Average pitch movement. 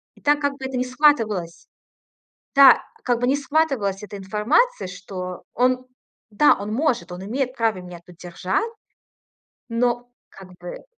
No: wide, 5.9 semitones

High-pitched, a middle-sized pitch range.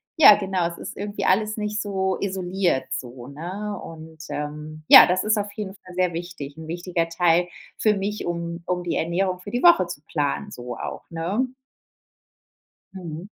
No: medium, 180 Hz; average, 3.7 semitones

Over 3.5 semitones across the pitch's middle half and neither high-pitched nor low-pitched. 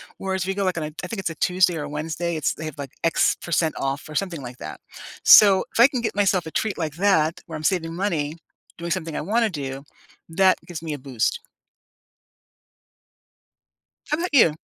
Yes: average, 3.9 semitones; medium, 170 Hz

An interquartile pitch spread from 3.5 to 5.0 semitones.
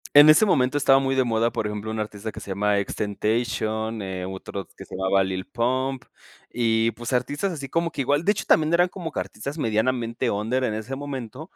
Yes: average, 4.4 semitones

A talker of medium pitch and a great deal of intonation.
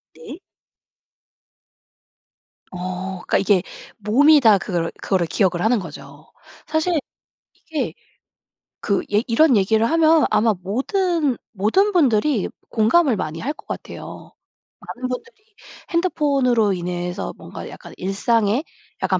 No: high, 225 Hz; wide, 7.8 semitones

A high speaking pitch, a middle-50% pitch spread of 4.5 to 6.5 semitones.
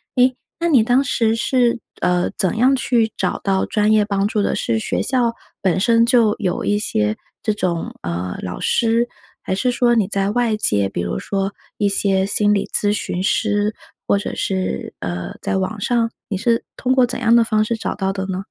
No: high, 210 Hz; average, 3.6 semitones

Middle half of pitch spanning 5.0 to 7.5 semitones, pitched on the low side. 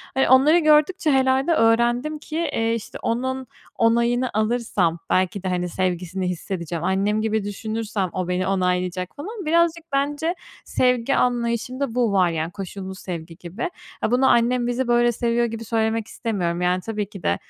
No: wide, 5.4 semitones; high, 225 Hz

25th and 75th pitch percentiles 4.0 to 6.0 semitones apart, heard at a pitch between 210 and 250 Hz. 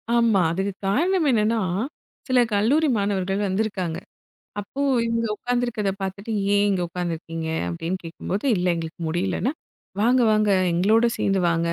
No: average, 4.3 semitones; high, 200 Hz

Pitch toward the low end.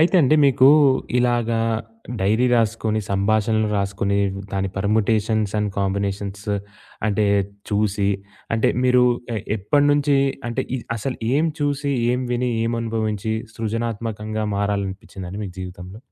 Yes: low, 110 Hz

